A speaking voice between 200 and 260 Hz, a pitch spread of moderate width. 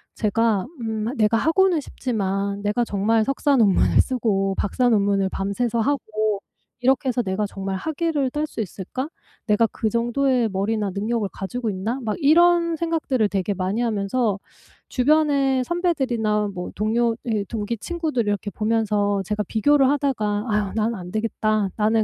Yes: high, 225 Hz; average, 4.1 semitones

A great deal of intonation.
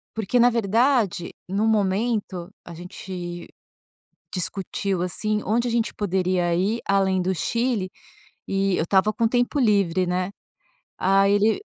No: average, 3.2 semitones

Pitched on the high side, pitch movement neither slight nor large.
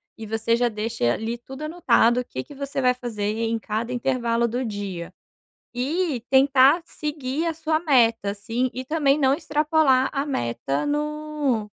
Yes: very high, 255 Hz; average, 4.5 semitones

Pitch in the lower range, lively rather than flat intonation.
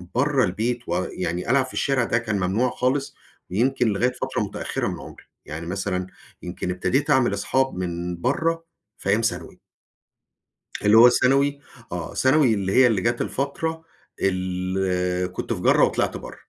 Yes: low, 115 Hz; wide, 6.2 semitones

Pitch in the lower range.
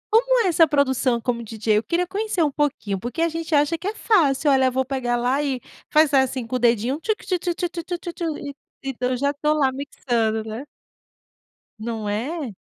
No: very high, 280 Hz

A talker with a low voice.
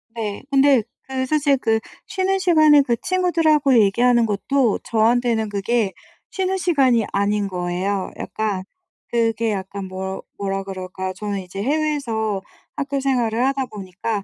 No: high, 230 Hz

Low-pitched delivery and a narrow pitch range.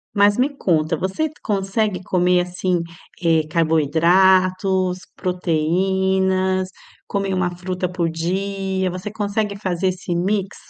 No: medium, 185 Hz; narrow, 1.6 semitones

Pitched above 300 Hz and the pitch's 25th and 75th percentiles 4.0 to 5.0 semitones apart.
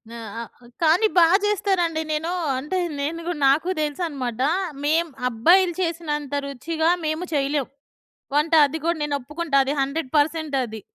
No: very high, 310 Hz; average, 3.0 semitones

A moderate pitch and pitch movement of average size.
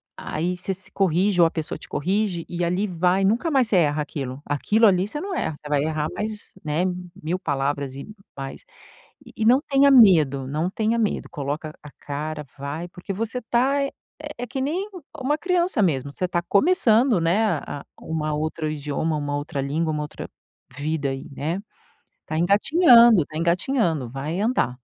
No: medium, 175 Hz; wide, 6.7 semitones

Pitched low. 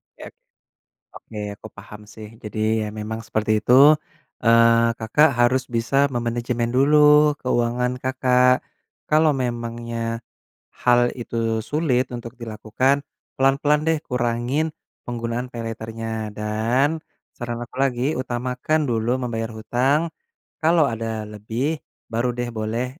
Yes: low, 120 Hz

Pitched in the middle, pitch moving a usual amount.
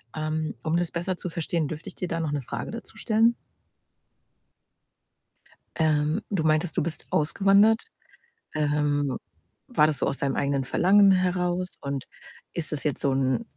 Yes: medium, 155 Hz; average, 3.6 semitones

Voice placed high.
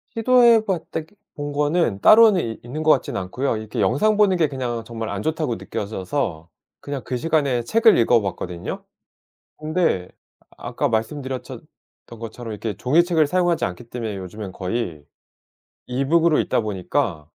No: low, 130 Hz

